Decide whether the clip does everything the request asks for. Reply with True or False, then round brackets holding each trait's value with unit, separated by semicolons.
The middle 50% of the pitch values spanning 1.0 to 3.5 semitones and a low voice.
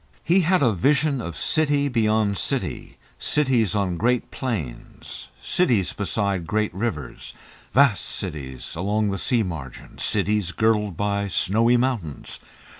False (5.3 semitones; 105 Hz)